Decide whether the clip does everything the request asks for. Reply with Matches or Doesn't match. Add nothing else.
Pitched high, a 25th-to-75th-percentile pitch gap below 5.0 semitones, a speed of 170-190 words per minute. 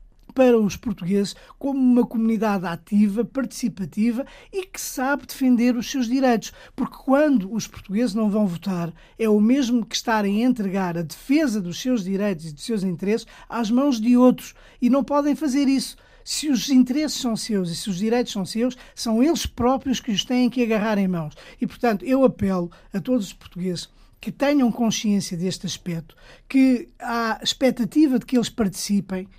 Matches